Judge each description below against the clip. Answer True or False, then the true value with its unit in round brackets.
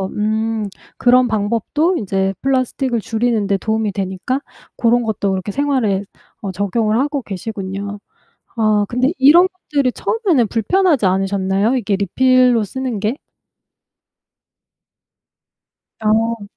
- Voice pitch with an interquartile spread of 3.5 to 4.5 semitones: True (4.1 semitones)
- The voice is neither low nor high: False (225 Hz)